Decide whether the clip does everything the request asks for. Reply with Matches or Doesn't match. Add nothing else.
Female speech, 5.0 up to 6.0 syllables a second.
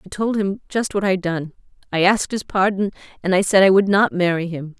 Matches